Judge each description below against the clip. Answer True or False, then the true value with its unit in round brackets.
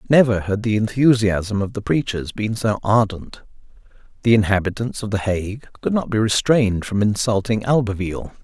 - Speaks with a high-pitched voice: False (105 Hz)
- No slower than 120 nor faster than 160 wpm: True (155 wpm)